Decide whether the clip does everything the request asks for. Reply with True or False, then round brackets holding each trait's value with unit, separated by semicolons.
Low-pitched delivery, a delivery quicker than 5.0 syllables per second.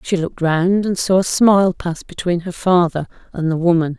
False (175 Hz; 5.2 syllables/s)